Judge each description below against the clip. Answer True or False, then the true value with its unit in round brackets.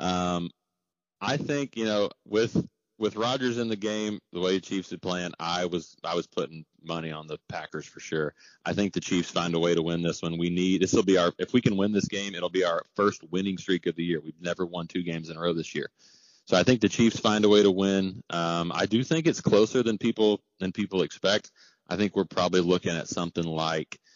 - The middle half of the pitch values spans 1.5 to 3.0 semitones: False (3.4 semitones)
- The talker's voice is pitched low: True (90 Hz)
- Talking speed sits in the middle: False (245 wpm)